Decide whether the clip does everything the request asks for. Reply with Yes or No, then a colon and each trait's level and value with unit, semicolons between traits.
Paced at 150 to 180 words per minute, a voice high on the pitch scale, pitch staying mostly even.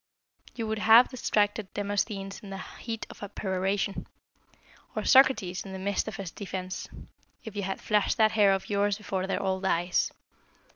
Yes: average, 175 wpm; high, 200 Hz; narrow, 2.1 semitones